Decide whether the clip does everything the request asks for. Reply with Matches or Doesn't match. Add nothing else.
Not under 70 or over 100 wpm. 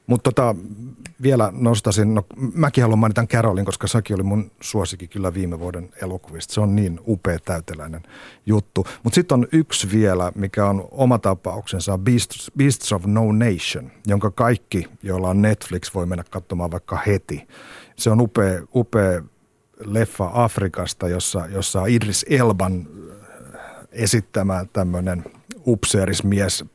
Doesn't match